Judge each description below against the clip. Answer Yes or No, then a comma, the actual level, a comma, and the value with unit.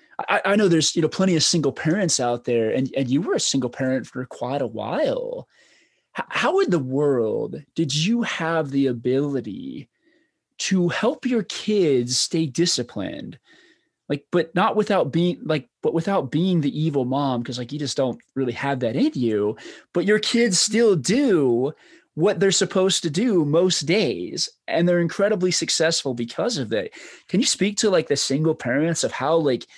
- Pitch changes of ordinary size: No, wide, 6.6 semitones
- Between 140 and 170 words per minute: No, average, 180 wpm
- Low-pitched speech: No, medium, 165 Hz